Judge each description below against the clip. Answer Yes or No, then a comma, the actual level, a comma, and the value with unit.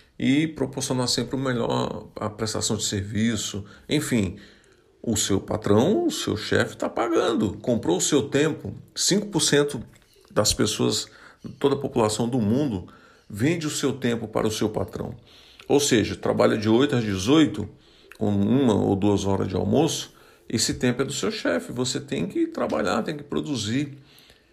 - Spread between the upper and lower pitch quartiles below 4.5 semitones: No, average, 5.3 semitones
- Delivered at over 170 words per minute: No, average, 160 wpm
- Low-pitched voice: Yes, low, 120 Hz